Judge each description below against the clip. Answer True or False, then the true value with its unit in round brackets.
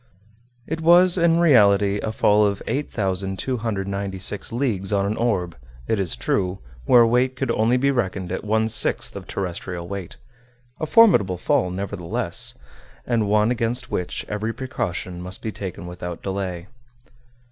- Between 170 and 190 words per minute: False (145 wpm)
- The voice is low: True (105 Hz)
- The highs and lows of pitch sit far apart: False (4.1 semitones)